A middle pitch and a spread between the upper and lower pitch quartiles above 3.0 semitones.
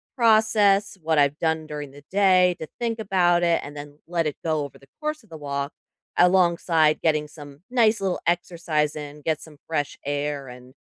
Yes: medium, 160 Hz; average, 4.0 semitones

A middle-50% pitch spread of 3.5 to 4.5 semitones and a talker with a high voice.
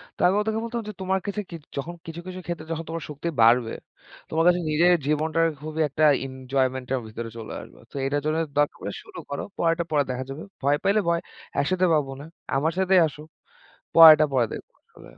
No: average, 4.1 semitones; medium, 155 Hz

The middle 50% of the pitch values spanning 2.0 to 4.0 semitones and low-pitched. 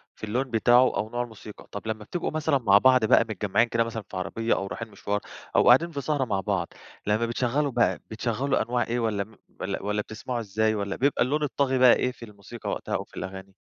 Yes: average, 3.5 semitones; low, 115 Hz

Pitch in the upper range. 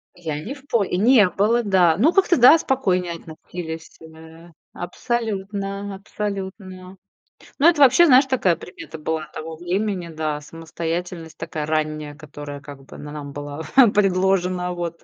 No: medium, 180 Hz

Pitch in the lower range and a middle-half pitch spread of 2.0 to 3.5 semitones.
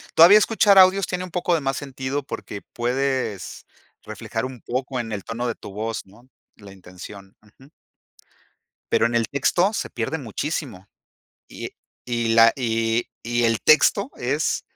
No: low, 120 Hz; average, 4.3 semitones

